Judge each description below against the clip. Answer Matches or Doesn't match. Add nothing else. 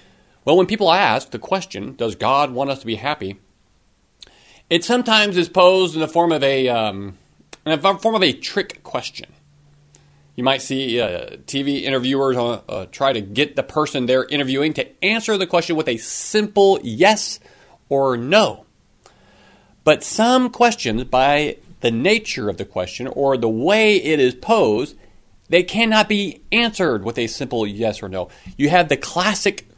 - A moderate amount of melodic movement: Doesn't match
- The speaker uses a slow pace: Doesn't match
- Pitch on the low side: Doesn't match